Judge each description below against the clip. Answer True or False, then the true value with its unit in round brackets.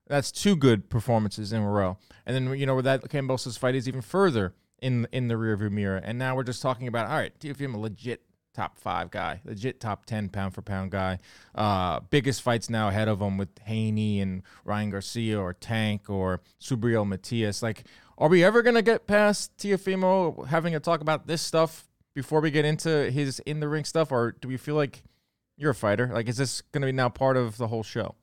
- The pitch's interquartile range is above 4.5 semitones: True (5.6 semitones)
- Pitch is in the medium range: False (120 Hz)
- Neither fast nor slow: False (215 wpm)